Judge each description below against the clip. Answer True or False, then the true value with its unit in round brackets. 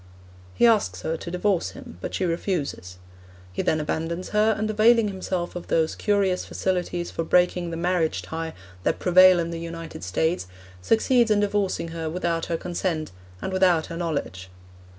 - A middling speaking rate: True (170 wpm)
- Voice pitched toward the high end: False (175 Hz)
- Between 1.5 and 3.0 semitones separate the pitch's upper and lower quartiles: True (2.7 semitones)